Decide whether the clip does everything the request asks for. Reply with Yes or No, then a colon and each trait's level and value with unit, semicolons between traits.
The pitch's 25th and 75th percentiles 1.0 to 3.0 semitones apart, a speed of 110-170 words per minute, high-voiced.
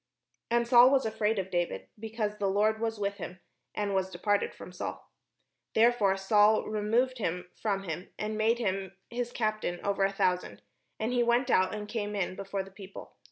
No: narrow, 2.6 semitones; average, 185 wpm; high, 210 Hz